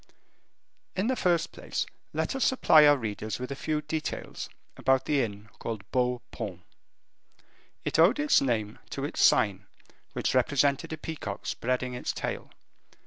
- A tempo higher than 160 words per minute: No, average, 150 wpm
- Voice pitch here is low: Yes, low, 130 Hz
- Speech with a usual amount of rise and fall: No, wide, 6.1 semitones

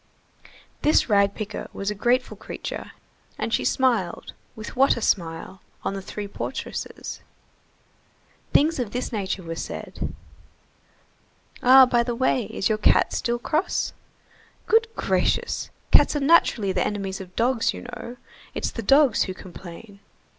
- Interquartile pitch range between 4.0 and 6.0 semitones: Yes, average, 4.5 semitones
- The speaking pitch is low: No, high, 225 Hz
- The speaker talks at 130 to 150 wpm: Yes, average, 145 wpm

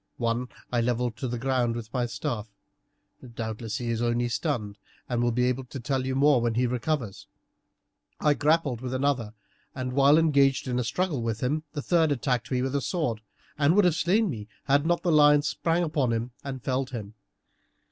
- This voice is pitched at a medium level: No, low, 130 Hz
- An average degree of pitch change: Yes, average, 3.8 semitones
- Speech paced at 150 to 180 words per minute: No, average, 200 wpm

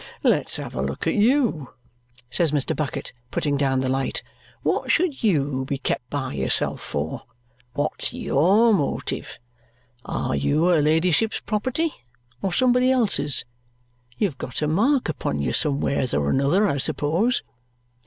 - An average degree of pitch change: No, wide, 7.9 semitones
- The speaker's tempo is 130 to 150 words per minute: Yes, average, 145 wpm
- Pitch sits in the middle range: Yes, medium, 155 Hz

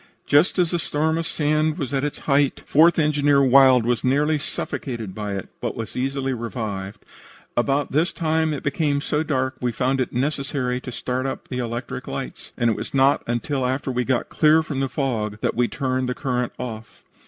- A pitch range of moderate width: Yes, average, 3.1 semitones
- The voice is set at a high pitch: No, low, 135 Hz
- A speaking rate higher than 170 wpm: Yes, average, 200 wpm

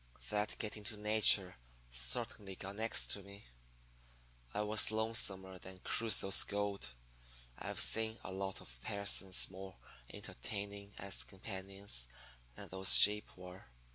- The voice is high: No, low, 100 Hz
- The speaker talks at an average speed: No, slow, 130 wpm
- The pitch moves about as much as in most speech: No, narrow, 1.9 semitones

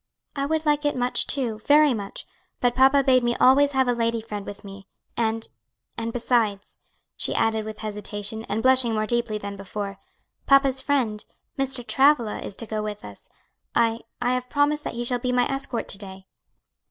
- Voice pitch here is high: Yes, high, 235 Hz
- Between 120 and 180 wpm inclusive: No, average, 190 wpm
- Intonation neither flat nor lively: Yes, average, 3.7 semitones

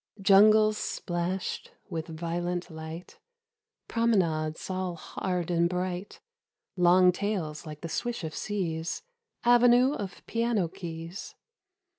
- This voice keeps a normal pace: No, slow, 105 wpm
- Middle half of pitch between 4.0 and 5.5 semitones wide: No, average, 3.6 semitones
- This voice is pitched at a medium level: Yes, medium, 180 Hz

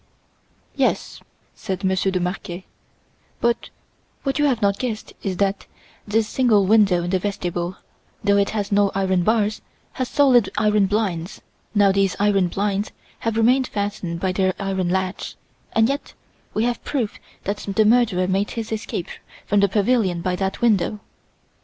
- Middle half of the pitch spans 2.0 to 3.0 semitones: Yes, average, 2.7 semitones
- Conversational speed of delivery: Yes, average, 160 wpm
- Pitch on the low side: No, high, 200 Hz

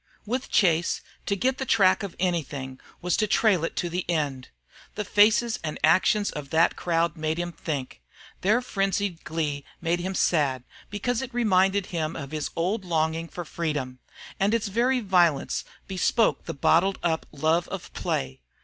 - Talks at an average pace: Yes, average, 165 wpm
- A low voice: No, medium, 175 Hz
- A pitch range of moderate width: Yes, average, 4.3 semitones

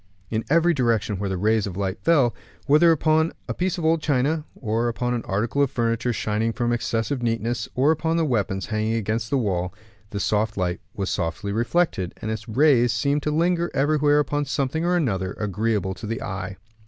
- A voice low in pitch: Yes, low, 115 Hz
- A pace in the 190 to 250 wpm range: Yes, average, 195 wpm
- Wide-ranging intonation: Yes, wide, 5.8 semitones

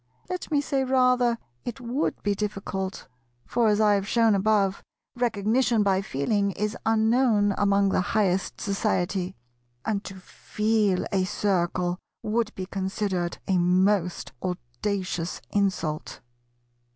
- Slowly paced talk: Yes, slow, 125 wpm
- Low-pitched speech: No, high, 200 Hz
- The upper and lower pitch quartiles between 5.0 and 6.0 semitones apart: No, average, 2.8 semitones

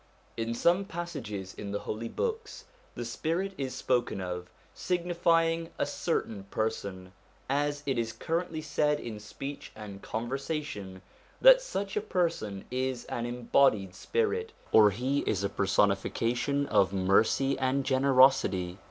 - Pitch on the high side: No, low, 130 Hz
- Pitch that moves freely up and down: Yes, wide, 8.0 semitones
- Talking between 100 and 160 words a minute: Yes, slow, 135 wpm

